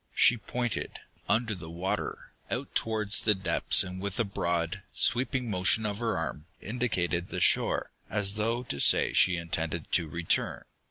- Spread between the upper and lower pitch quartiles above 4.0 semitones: Yes, average, 4.5 semitones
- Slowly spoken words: No, average, 165 wpm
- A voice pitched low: Yes, low, 100 Hz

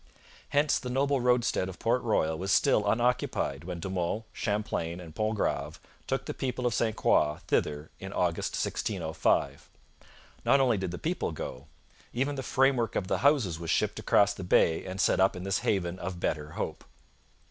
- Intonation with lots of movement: Yes, wide, 6.4 semitones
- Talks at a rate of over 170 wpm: Yes, average, 180 wpm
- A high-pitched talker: No, low, 100 Hz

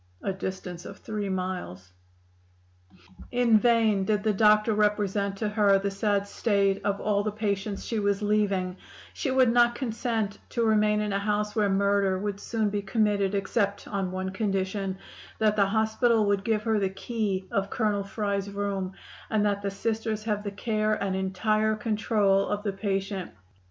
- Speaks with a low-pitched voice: No, high, 205 Hz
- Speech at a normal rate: Yes, average, 170 wpm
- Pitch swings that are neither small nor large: No, narrow, 1.6 semitones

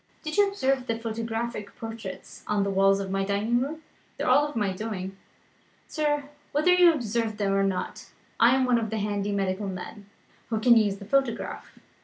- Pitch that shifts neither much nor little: Yes, average, 4.4 semitones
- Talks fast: No, average, 190 wpm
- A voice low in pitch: No, high, 225 Hz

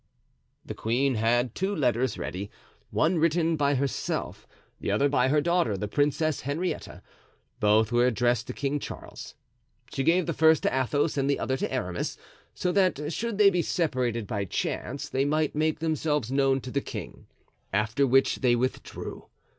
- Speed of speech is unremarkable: Yes, average, 170 wpm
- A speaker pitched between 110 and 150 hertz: Yes, medium, 140 Hz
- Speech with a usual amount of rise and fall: Yes, average, 4.5 semitones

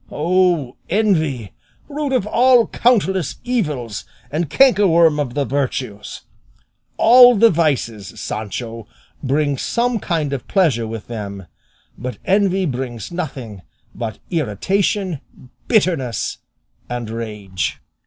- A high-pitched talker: No, medium, 150 Hz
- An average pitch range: No, wide, 8.7 semitones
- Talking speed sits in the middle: No, slow, 105 wpm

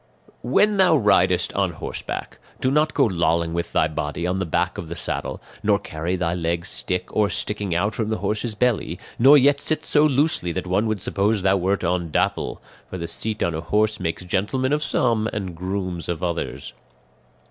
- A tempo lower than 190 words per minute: No, average, 195 wpm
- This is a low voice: Yes, very low, 95 Hz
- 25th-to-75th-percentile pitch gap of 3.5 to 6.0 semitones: Yes, average, 4.4 semitones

